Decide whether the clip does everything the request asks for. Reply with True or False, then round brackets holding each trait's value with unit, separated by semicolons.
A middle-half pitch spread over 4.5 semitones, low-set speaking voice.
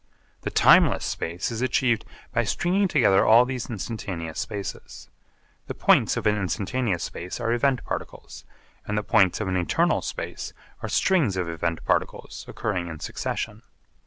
True (5.0 semitones; 105 Hz)